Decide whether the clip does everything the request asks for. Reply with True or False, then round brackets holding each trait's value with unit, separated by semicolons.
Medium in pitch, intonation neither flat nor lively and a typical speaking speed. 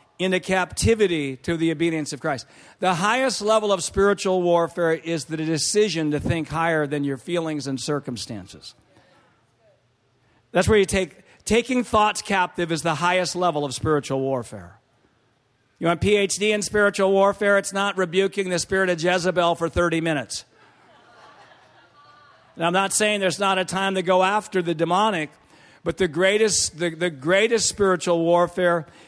True (175 Hz; 3.5 semitones; 155 wpm)